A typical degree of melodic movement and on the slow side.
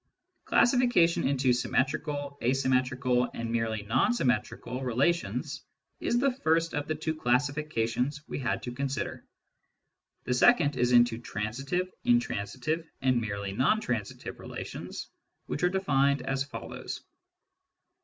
Yes: average, 4.5 semitones; slow, 125 wpm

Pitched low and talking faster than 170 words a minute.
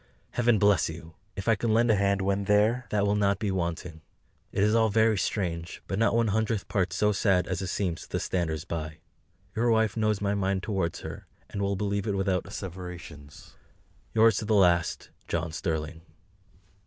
Yes: low, 100 Hz; average, 190 wpm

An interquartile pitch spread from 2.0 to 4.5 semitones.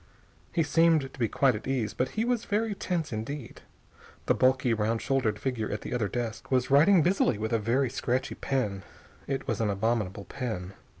Yes: average, 4.2 semitones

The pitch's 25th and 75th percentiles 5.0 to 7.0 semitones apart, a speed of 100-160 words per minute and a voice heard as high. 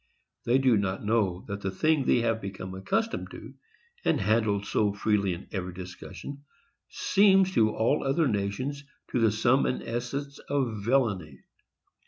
No: average, 5.3 semitones; average, 150 wpm; low, 110 Hz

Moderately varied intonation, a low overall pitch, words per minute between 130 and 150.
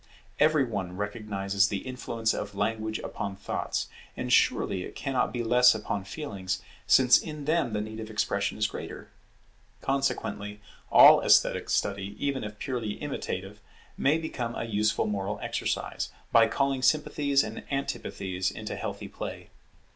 Yes: average, 4.6 semitones; low, 110 Hz; average, 145 wpm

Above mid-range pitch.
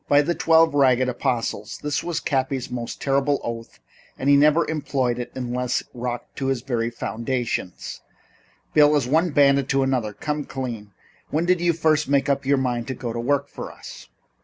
No: low, 135 Hz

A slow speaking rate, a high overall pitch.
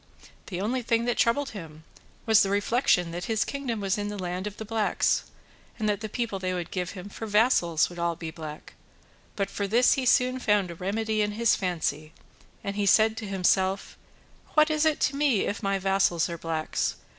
No: fast, 205 wpm; high, 205 Hz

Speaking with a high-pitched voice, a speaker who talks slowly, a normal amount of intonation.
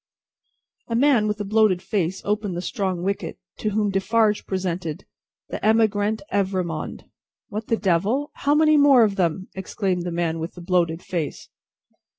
No: high, 195 Hz; average, 160 wpm; average, 3.5 semitones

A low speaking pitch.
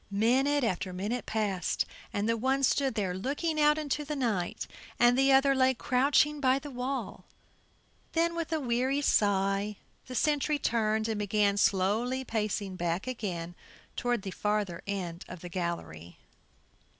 No: high, 230 Hz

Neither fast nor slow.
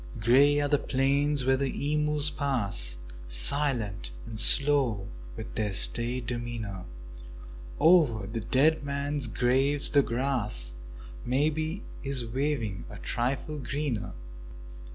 No: slow, 110 wpm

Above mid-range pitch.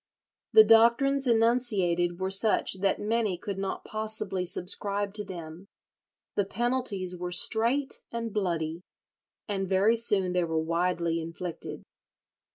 Yes: high, 195 Hz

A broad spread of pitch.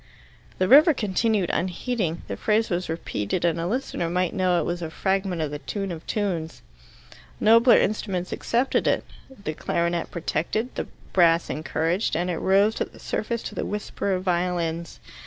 No: average, 3.8 semitones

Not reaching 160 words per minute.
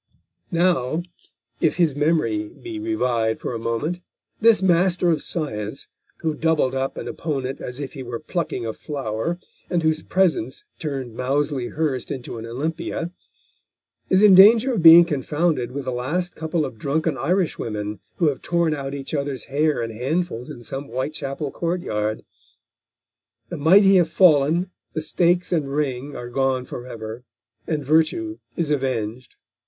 Yes: average, 150 wpm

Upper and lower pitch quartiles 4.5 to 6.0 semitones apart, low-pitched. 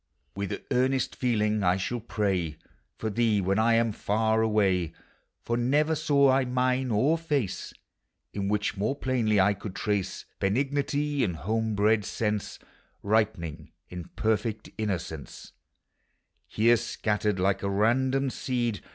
No: average, 4.0 semitones; low, 110 Hz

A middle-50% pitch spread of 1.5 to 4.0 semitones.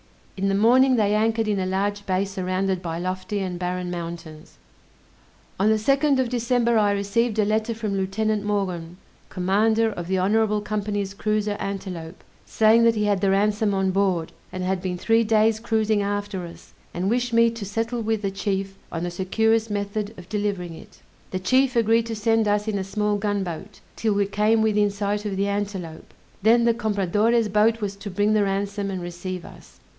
Yes: narrow, 2.4 semitones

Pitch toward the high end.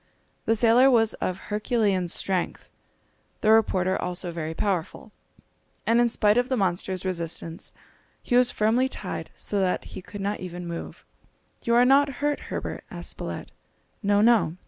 Yes: high, 205 Hz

